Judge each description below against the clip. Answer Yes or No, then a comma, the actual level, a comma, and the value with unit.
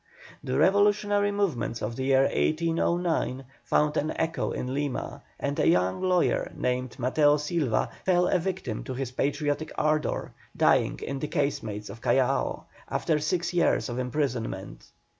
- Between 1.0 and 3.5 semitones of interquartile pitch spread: No, average, 5.1 semitones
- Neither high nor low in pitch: Yes, medium, 145 Hz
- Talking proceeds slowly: No, average, 145 wpm